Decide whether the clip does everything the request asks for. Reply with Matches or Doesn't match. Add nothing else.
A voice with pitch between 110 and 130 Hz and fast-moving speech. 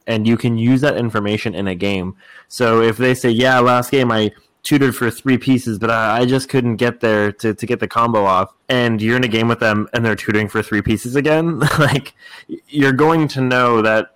Matches